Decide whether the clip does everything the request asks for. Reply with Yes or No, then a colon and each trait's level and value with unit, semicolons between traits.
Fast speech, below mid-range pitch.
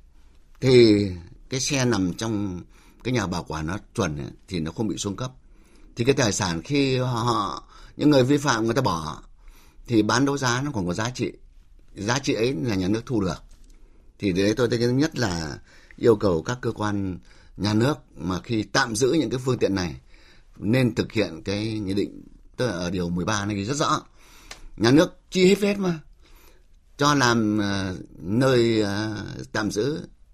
No: average, 190 wpm; low, 110 Hz